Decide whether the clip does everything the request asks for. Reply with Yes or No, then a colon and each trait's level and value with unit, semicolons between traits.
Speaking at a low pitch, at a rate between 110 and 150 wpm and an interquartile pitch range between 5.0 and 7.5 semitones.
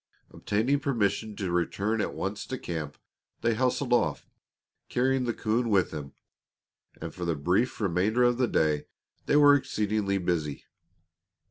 Yes: low, 105 Hz; average, 145 wpm; wide, 5.5 semitones